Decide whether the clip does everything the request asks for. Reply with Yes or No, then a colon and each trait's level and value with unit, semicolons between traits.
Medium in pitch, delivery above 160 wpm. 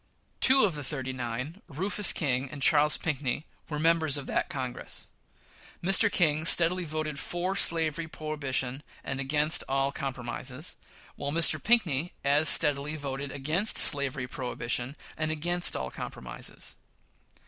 No: medium, 150 Hz; slow, 135 wpm